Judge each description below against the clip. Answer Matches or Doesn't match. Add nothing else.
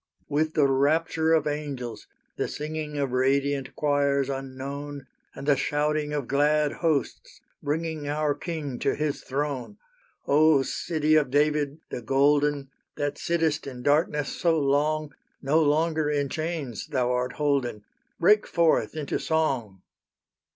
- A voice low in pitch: Doesn't match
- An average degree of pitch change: Doesn't match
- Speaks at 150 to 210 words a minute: Doesn't match